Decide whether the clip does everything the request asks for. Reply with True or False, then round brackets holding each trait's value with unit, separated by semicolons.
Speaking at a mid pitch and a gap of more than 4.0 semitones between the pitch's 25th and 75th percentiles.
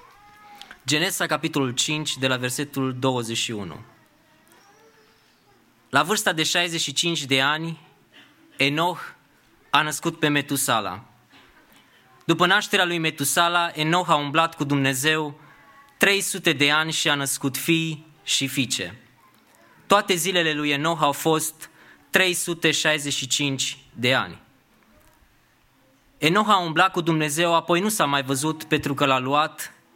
False (155 Hz; 3.7 semitones)